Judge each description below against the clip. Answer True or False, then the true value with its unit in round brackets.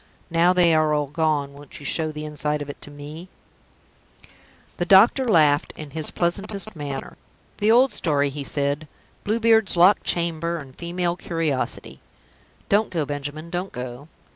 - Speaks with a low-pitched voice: False (160 Hz)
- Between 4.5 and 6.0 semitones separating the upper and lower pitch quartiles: False (3.6 semitones)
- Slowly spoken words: False (160 wpm)